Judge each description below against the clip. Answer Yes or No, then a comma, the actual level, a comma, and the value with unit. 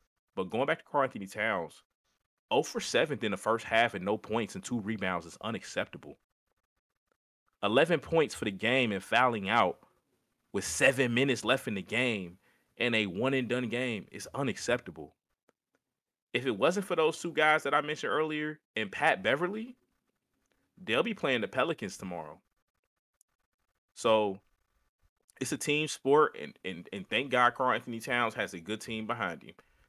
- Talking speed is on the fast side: No, average, 170 wpm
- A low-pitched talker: Yes, low, 120 Hz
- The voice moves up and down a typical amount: No, wide, 5.7 semitones